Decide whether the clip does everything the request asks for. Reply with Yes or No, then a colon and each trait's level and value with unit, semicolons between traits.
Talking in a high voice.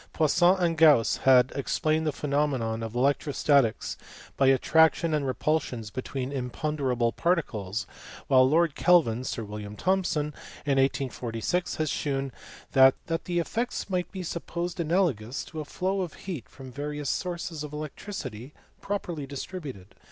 No: medium, 145 Hz